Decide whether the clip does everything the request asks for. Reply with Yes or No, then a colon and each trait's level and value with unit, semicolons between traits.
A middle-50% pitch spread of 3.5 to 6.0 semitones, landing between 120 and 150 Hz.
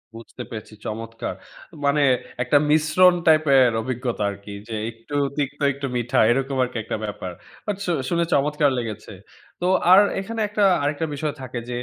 Yes: average, 5.0 semitones; low, 135 Hz